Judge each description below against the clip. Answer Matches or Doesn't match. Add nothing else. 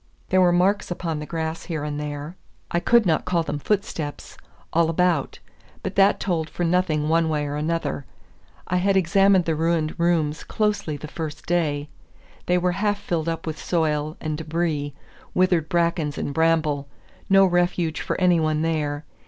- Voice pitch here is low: Doesn't match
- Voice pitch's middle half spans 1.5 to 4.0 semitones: Matches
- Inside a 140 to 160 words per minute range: Doesn't match